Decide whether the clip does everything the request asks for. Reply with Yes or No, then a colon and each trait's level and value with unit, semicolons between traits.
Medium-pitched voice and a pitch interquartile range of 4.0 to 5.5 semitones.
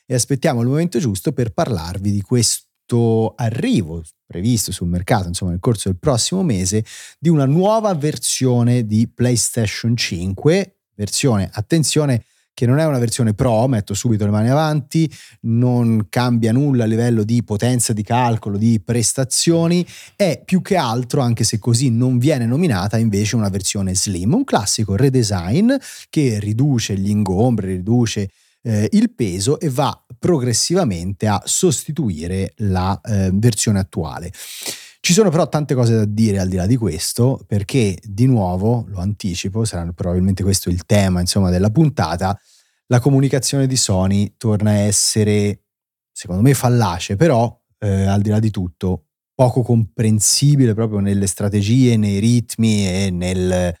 No: low, 115 Hz; average, 4.3 semitones